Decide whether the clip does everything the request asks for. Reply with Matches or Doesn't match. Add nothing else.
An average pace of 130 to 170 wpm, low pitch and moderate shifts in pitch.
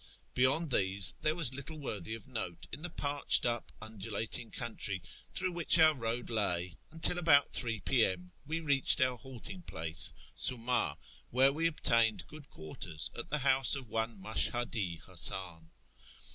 Doesn't match